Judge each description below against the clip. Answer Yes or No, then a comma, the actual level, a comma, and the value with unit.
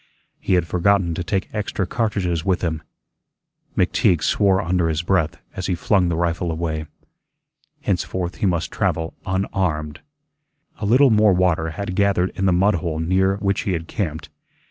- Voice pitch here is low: Yes, very low, 90 Hz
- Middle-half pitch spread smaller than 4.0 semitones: Yes, average, 2.9 semitones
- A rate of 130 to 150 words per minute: No, average, 165 wpm